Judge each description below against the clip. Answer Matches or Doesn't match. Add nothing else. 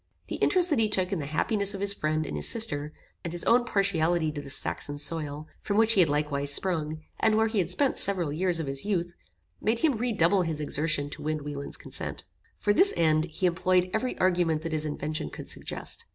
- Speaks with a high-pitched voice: Doesn't match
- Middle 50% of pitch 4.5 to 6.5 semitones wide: Matches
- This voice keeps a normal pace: Doesn't match